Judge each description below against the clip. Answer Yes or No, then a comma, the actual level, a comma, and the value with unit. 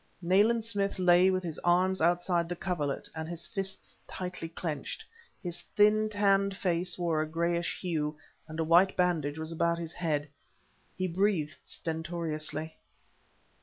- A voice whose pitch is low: No, medium, 175 Hz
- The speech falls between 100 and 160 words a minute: Yes, average, 145 wpm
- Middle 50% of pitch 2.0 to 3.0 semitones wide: Yes, narrow, 2.6 semitones